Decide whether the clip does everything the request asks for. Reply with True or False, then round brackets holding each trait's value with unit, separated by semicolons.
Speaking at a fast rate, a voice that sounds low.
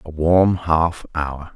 False (155 wpm; 80 Hz)